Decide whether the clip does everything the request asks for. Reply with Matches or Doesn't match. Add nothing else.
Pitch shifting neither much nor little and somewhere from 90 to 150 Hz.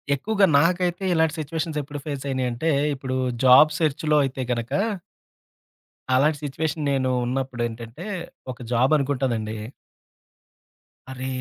Matches